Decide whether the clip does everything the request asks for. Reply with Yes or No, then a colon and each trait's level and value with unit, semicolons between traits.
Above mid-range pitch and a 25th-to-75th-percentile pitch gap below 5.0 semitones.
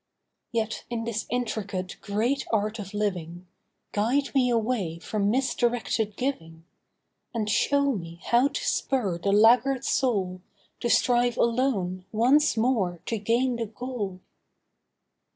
Yes: high, 225 Hz; average, 3.9 semitones